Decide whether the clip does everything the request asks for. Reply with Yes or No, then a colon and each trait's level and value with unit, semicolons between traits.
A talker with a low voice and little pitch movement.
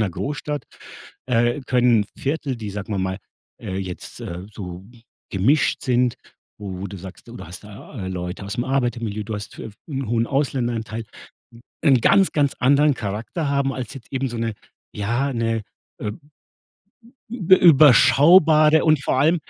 No: low, 120 Hz; average, 5.3 semitones